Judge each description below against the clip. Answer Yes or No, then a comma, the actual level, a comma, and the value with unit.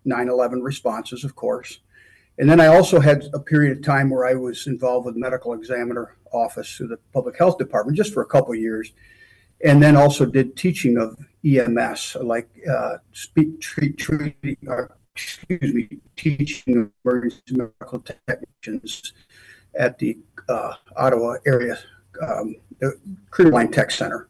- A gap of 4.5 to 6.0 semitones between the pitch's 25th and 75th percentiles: No, average, 3.2 semitones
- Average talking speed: Yes, average, 160 wpm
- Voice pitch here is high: No, low, 130 Hz